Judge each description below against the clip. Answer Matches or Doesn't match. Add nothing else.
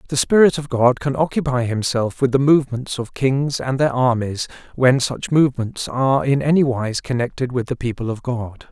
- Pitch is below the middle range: Matches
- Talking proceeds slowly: Doesn't match